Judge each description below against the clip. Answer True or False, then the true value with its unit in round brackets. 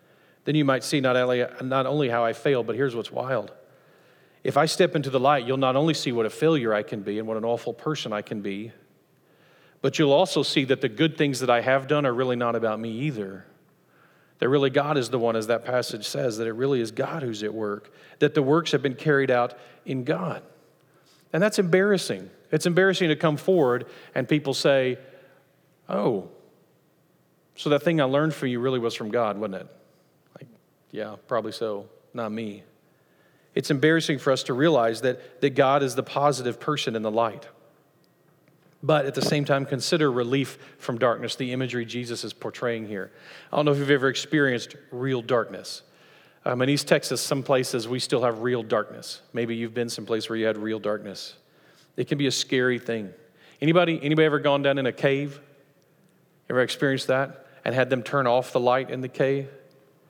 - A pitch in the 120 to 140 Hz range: True (135 Hz)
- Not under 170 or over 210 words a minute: True (200 wpm)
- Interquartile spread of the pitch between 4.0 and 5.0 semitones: False (3.6 semitones)